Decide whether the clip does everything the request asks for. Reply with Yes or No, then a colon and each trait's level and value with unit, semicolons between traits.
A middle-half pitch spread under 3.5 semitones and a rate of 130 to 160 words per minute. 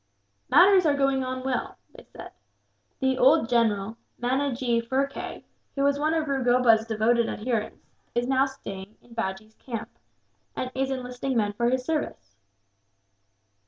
Yes: average, 2.9 semitones; average, 140 wpm